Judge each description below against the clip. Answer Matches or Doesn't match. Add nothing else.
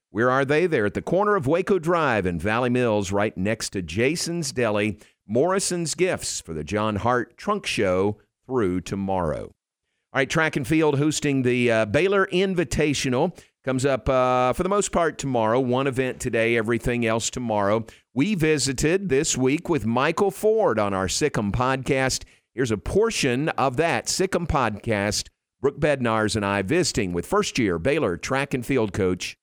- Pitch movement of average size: Doesn't match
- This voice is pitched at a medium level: Doesn't match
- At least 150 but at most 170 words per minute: Matches